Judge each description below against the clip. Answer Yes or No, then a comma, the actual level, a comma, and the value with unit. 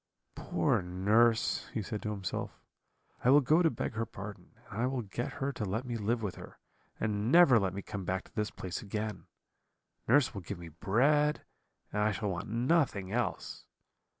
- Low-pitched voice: Yes, low, 110 Hz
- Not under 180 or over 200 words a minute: Yes, average, 190 wpm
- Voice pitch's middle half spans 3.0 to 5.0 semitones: Yes, average, 3.7 semitones